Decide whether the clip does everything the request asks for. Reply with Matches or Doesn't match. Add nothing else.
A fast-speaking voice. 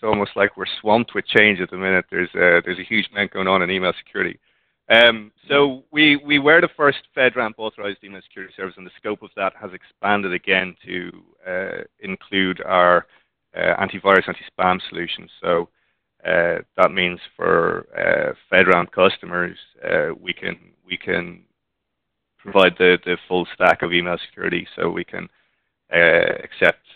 Doesn't match